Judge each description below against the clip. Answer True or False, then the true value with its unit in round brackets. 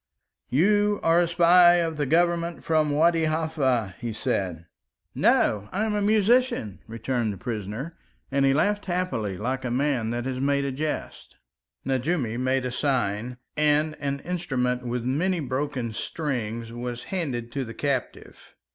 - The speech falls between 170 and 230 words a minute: False (155 wpm)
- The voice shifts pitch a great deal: True (5.7 semitones)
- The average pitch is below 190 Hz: True (135 Hz)